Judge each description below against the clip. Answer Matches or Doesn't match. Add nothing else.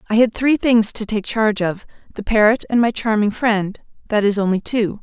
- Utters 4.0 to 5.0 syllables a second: Doesn't match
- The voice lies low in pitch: Doesn't match